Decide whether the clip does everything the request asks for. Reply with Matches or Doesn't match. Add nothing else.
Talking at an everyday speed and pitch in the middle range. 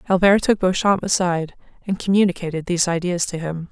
Matches